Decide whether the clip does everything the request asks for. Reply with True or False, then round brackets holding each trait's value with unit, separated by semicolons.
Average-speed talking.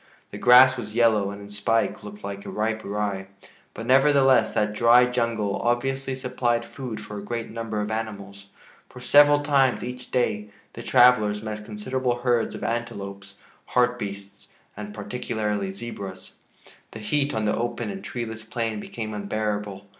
True (155 wpm)